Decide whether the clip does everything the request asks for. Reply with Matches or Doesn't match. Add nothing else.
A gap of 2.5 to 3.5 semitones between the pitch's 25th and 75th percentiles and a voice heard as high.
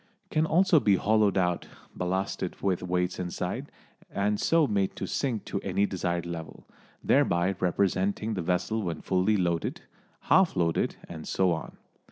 Doesn't match